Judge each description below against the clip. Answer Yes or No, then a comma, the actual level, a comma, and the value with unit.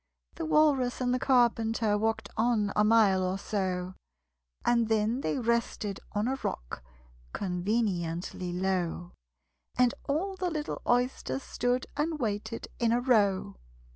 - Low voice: No, high, 225 Hz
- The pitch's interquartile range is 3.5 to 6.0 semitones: Yes, average, 4.4 semitones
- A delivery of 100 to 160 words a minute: Yes, slow, 135 wpm